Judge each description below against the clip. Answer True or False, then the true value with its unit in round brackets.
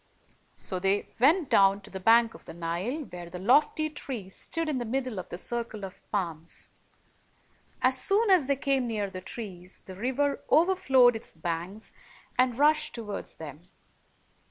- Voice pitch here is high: True (230 Hz)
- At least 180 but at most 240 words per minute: False (165 wpm)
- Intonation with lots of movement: True (6.5 semitones)